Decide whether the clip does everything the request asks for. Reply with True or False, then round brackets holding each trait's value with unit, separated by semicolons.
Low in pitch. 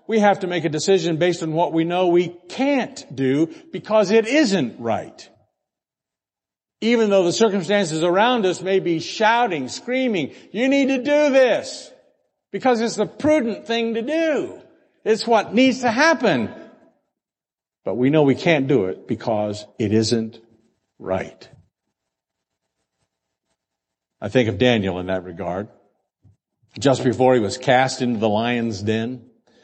False (175 Hz)